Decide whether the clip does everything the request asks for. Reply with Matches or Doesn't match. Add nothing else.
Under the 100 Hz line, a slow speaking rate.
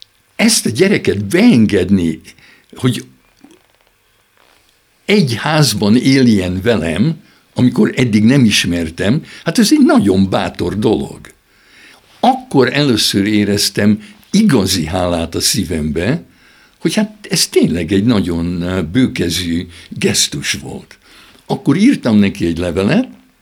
Doesn't match